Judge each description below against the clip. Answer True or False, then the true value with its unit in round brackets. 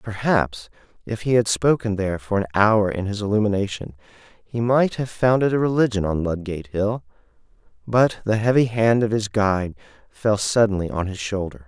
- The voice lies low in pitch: True (105 Hz)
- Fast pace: False (170 wpm)